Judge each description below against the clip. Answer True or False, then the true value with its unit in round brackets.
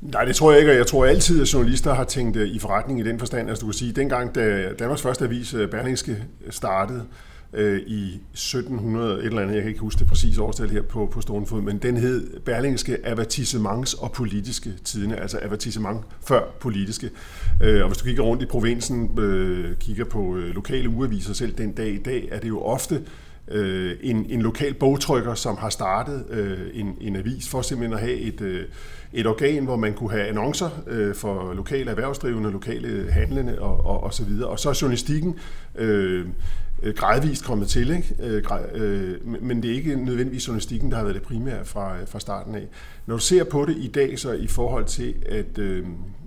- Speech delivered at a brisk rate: False (195 wpm)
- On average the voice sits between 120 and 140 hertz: False (110 Hz)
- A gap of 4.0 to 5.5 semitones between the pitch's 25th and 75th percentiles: False (3.5 semitones)